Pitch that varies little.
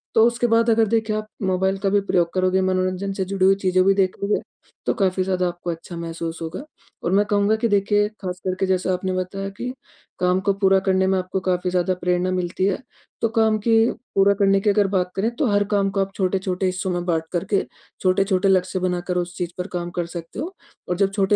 Yes: narrow, 1.8 semitones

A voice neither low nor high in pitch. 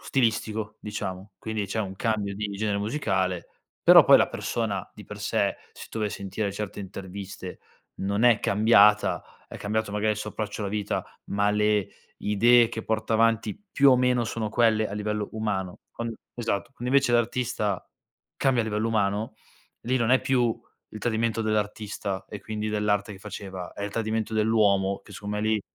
No: low, 105 Hz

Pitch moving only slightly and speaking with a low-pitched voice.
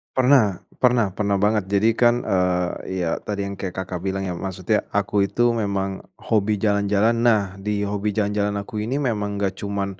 Yes: narrow, 1.8 semitones; low, 100 Hz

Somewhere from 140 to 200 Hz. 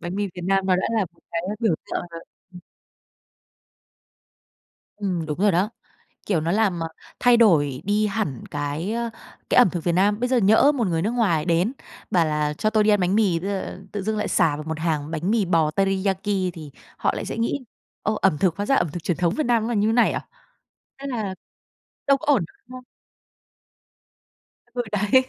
Yes: high, 195 Hz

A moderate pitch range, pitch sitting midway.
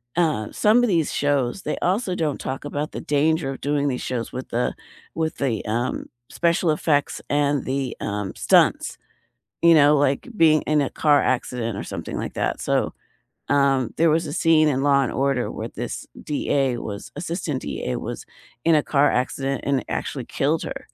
Yes: average, 3.3 semitones; medium, 145 Hz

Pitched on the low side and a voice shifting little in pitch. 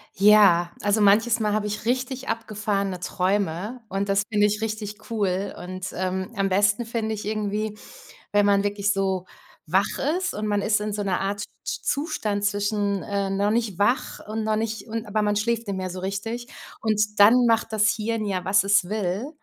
No: high, 205 Hz; narrow, 1.7 semitones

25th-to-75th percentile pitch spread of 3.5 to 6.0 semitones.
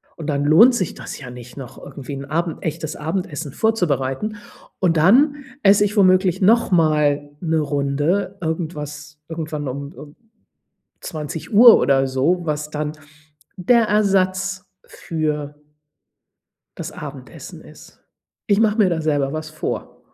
Yes: average, 4.5 semitones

